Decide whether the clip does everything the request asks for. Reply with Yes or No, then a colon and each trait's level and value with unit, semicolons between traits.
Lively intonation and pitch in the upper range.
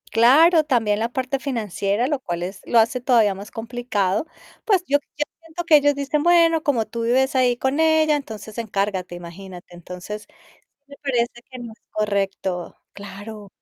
Yes: wide, 5.8 semitones; high, 235 Hz